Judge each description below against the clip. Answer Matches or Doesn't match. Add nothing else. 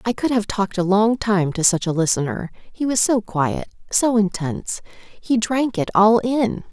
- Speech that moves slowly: Doesn't match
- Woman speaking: Matches